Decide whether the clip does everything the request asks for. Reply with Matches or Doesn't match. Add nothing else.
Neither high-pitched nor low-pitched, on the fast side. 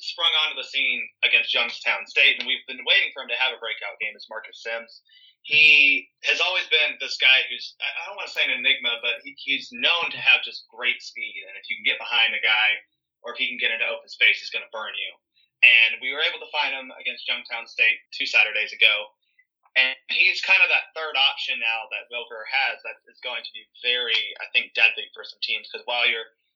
Matches